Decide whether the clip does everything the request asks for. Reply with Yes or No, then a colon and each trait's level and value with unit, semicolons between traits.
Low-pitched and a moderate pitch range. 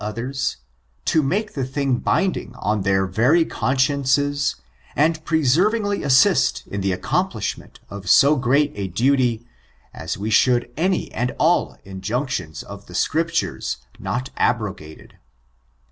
No: low, 130 Hz; wide, 6.3 semitones